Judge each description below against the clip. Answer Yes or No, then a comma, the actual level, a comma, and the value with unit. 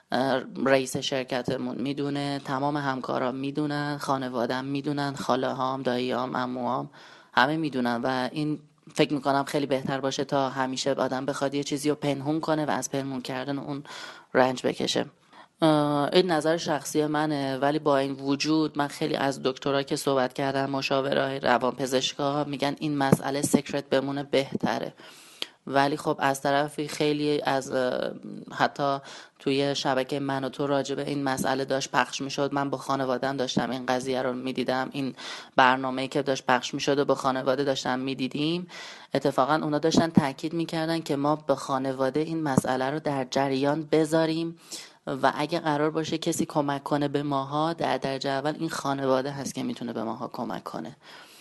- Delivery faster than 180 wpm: No, average, 160 wpm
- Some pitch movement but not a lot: No, narrow, 1.9 semitones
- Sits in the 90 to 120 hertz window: No, medium, 140 Hz